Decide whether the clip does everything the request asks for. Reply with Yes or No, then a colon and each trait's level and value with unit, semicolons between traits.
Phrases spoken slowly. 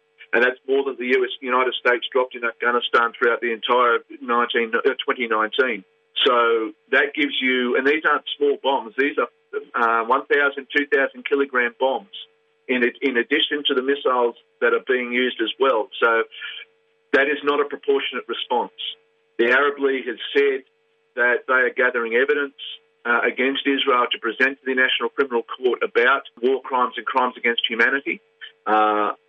No: average, 160 wpm